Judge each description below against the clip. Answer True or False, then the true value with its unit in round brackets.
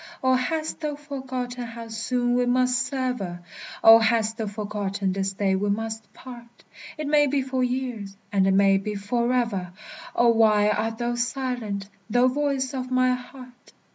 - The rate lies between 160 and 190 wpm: True (165 wpm)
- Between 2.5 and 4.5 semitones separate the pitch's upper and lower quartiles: True (3.4 semitones)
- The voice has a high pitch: True (240 Hz)